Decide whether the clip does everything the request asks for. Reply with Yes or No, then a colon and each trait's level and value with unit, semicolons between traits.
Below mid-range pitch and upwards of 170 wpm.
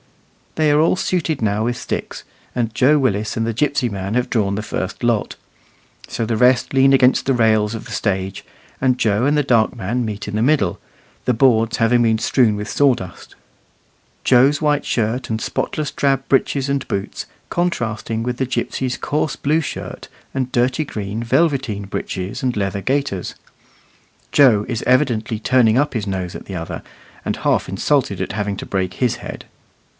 Yes: low, 120 Hz; average, 180 wpm